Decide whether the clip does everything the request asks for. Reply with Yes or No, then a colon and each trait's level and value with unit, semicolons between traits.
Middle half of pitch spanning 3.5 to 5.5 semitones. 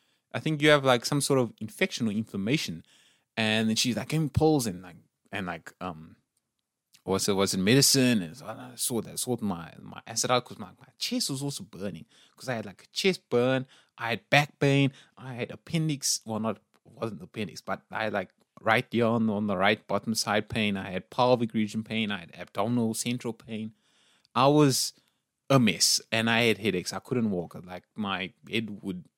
Yes: average, 3.8 semitones